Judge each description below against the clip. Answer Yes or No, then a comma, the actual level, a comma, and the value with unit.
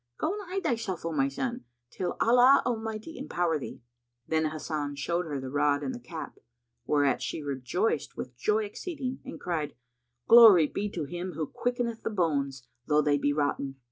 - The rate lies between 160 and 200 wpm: Yes, average, 175 wpm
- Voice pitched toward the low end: No, medium, 165 Hz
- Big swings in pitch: Yes, wide, 7.8 semitones